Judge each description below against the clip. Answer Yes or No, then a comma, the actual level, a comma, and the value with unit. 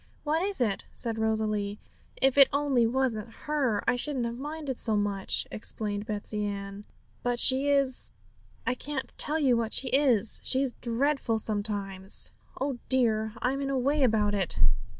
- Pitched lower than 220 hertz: No, high, 240 Hz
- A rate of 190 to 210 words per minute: No, average, 165 wpm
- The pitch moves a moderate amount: Yes, average, 4.3 semitones